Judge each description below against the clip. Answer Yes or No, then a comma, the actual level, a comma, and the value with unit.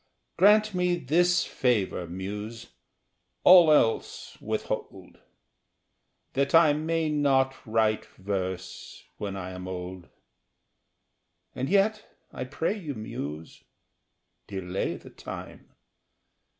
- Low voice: Yes, low, 125 Hz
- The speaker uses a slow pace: Yes, slow, 100 wpm